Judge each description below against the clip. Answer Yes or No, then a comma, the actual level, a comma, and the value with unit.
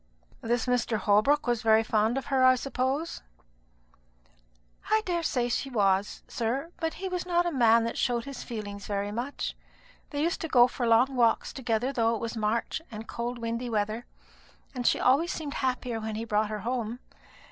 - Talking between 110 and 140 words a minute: No, average, 185 wpm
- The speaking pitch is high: Yes, high, 240 Hz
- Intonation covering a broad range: No, average, 3.3 semitones